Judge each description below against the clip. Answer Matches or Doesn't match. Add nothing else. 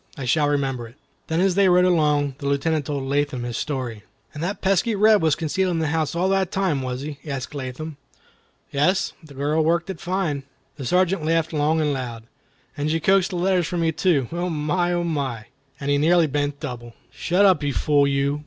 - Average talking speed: Doesn't match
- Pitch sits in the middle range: Matches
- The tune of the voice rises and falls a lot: Doesn't match